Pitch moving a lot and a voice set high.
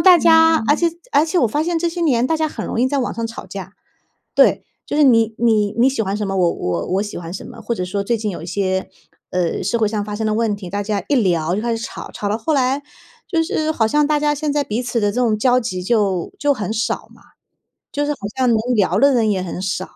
Yes: wide, 6.0 semitones; high, 225 Hz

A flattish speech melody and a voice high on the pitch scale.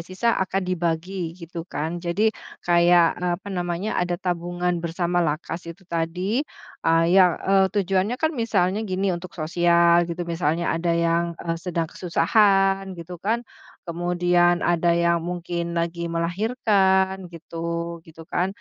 No: narrow, 2.0 semitones; medium, 175 Hz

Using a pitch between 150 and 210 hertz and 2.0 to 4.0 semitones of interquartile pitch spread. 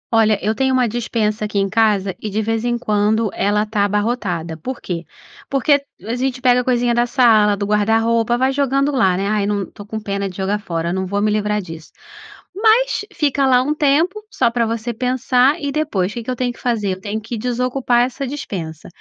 No: high, 225 Hz; average, 3.6 semitones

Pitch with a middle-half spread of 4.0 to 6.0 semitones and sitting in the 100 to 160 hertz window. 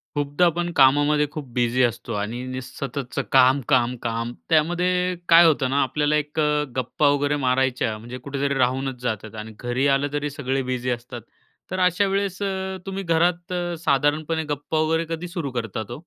Yes: average, 4.3 semitones; medium, 140 Hz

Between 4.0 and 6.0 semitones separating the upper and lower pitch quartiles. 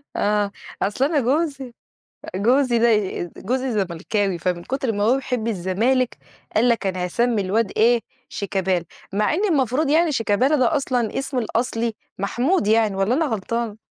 Yes: average, 4.3 semitones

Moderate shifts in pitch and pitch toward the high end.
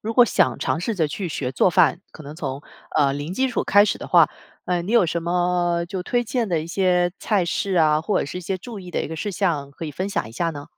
No: average, 3.8 semitones; medium, 175 Hz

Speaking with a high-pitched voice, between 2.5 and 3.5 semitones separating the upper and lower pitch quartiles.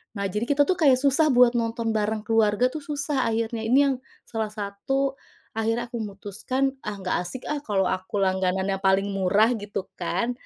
No: high, 225 Hz; average, 4.3 semitones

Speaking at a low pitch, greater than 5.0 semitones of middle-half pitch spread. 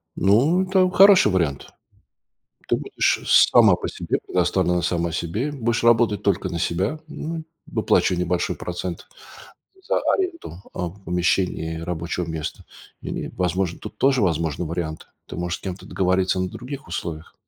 Yes: very low, 90 Hz; wide, 5.5 semitones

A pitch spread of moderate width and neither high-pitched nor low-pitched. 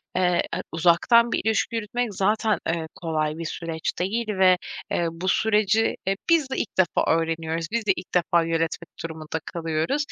Yes: average, 4.9 semitones; medium, 180 Hz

